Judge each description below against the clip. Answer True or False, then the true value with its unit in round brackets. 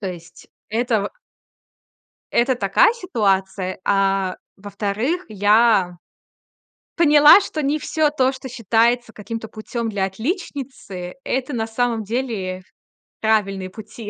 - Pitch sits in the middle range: False (220 Hz)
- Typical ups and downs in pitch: True (4.7 semitones)